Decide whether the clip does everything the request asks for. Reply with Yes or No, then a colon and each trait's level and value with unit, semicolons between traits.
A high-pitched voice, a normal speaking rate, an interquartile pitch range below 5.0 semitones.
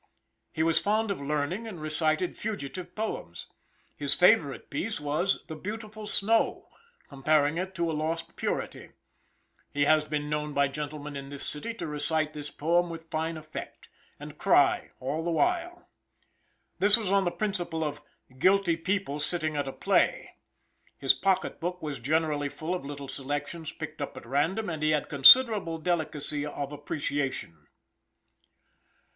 No: medium, 155 Hz; average, 155 wpm; average, 4.0 semitones